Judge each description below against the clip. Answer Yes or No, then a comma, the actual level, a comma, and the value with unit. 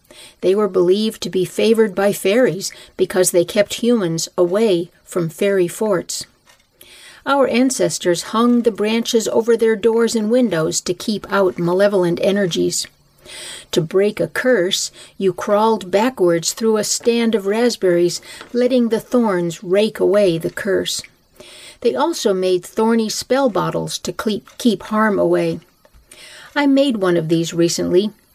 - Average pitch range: Yes, average, 4.2 semitones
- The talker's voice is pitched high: Yes, high, 200 Hz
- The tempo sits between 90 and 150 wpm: Yes, average, 140 wpm